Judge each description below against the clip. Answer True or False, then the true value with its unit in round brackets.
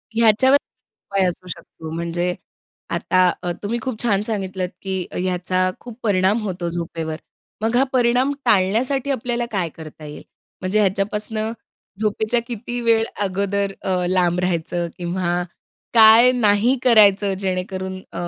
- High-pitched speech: True (195 Hz)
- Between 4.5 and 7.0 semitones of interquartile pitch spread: False (3.7 semitones)